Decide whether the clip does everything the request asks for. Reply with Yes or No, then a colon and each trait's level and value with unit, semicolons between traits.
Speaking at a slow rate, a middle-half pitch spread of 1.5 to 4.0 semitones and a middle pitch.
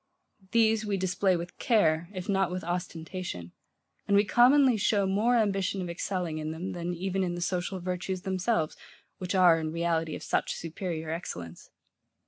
No: average, 165 wpm; narrow, 2.6 semitones; medium, 180 Hz